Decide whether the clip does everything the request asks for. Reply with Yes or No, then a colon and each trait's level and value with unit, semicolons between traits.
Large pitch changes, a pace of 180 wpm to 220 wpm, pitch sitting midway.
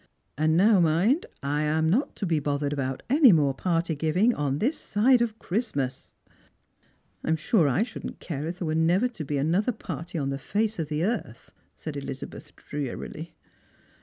Yes: wide, 6.0 semitones; average, 195 wpm; medium, 160 Hz